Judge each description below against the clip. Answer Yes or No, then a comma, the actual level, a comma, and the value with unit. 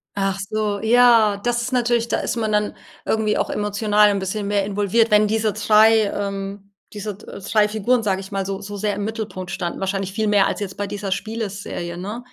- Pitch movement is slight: Yes, narrow, 1.8 semitones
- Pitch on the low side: No, high, 210 Hz